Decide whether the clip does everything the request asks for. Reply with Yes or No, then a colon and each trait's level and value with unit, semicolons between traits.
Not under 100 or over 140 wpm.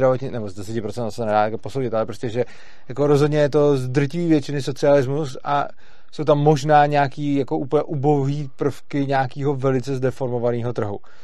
No: average, 160 wpm